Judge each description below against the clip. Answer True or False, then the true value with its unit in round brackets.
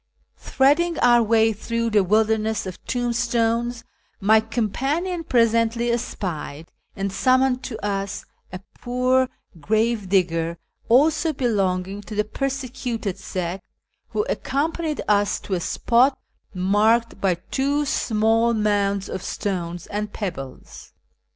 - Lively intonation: False (3.9 semitones)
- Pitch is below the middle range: False (220 Hz)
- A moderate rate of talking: False (115 wpm)